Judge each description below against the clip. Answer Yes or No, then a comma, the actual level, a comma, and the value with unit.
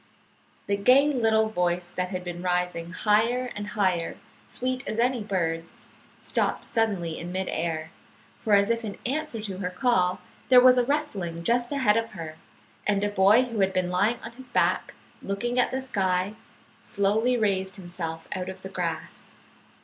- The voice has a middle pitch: No, high, 200 Hz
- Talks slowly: No, average, 170 wpm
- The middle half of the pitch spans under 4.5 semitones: No, average, 4.8 semitones